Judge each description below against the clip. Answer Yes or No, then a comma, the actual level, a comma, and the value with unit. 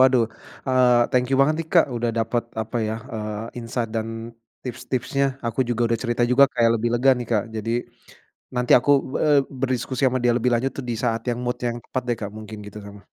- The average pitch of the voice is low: Yes, low, 120 Hz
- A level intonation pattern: Yes, narrow, 2.2 semitones